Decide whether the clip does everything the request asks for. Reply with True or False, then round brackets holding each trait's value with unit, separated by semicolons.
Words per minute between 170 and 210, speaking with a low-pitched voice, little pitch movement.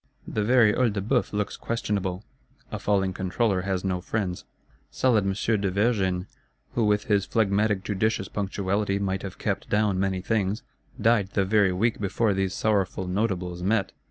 False (160 wpm; 100 Hz; 2.2 semitones)